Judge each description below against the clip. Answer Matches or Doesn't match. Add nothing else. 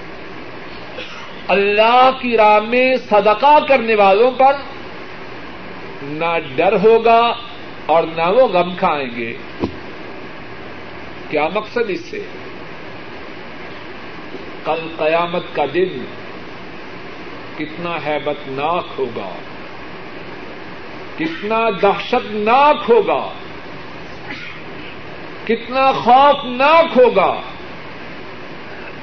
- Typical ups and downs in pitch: Doesn't match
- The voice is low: Doesn't match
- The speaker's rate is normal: Doesn't match